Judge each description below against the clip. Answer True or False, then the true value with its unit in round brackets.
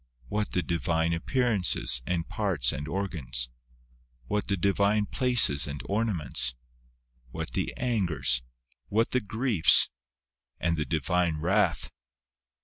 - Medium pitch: False (90 Hz)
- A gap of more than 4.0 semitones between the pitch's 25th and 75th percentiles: True (5.3 semitones)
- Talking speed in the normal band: False (115 wpm)